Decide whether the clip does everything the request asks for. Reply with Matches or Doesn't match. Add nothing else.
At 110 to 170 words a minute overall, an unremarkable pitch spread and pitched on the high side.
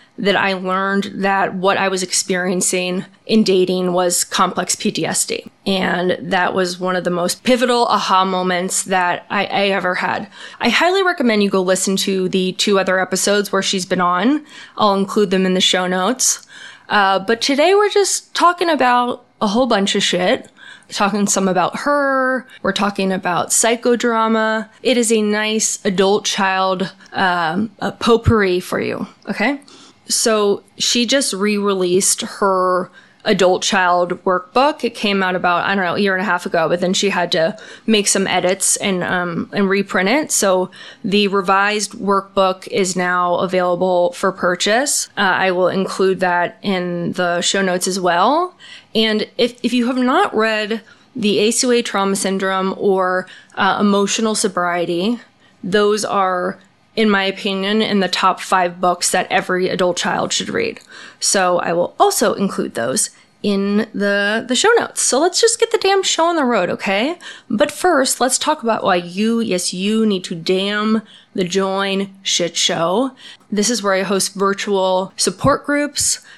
Matches